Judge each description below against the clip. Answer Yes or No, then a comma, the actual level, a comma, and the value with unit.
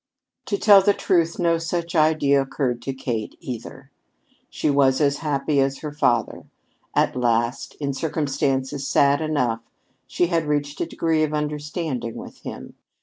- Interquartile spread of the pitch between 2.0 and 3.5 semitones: Yes, average, 2.9 semitones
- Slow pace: No, average, 150 wpm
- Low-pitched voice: No, medium, 145 Hz